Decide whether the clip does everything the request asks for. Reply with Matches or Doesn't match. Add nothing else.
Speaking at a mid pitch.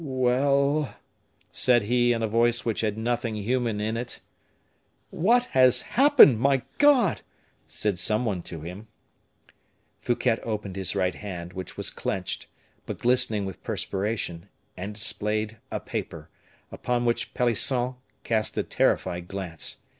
Doesn't match